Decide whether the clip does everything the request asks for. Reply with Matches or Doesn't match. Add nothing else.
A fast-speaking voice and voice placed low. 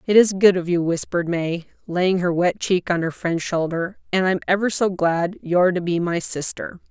Doesn't match